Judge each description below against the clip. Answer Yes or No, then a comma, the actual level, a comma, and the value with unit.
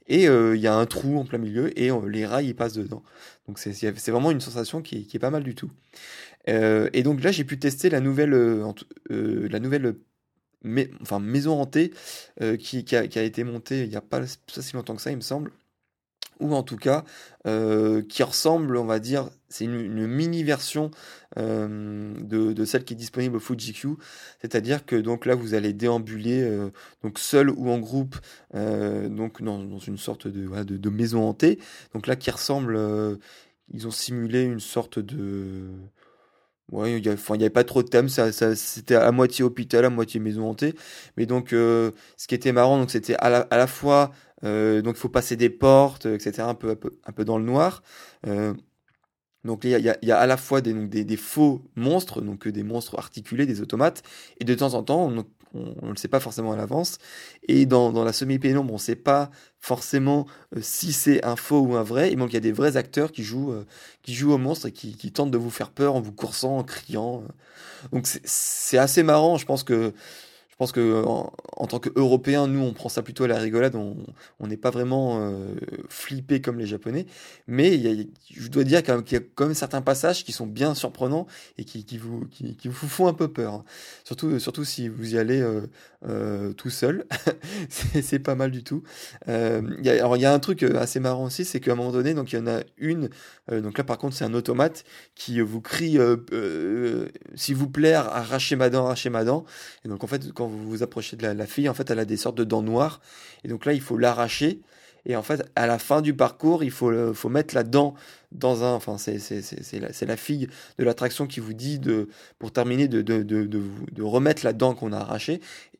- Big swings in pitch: No, average, 3.8 semitones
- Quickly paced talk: Yes, fast, 230 wpm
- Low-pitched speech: Yes, low, 120 Hz